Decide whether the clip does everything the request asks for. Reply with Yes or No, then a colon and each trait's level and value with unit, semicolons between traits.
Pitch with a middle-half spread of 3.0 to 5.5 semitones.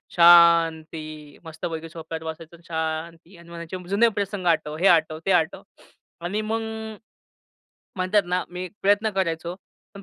No: narrow, 2.6 semitones